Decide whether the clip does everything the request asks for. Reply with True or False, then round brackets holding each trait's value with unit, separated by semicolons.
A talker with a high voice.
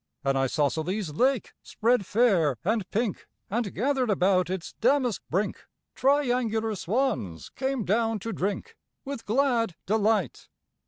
True (220 Hz)